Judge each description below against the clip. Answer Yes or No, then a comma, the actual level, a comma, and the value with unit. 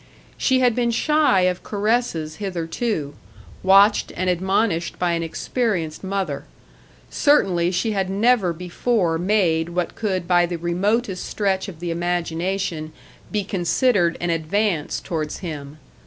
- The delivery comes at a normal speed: No, slow, 130 wpm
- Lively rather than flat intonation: No, average, 3.6 semitones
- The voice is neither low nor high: Yes, medium, 180 Hz